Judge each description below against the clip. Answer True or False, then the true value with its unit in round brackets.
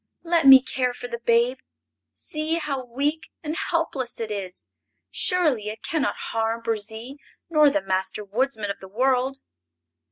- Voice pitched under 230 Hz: False (250 Hz)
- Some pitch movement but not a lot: True (4.9 semitones)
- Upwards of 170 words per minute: False (155 wpm)